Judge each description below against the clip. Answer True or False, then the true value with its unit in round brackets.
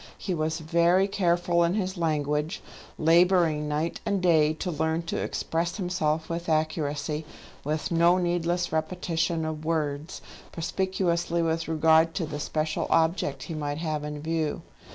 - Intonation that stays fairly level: True (2.0 semitones)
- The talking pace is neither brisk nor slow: True (145 wpm)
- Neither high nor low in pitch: True (165 Hz)